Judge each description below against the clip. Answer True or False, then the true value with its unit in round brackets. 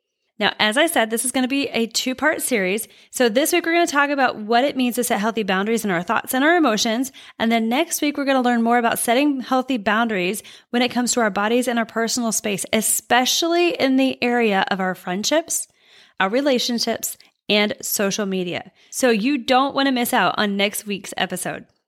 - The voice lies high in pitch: True (240 Hz)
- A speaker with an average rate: False (220 wpm)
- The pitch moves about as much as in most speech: True (3.8 semitones)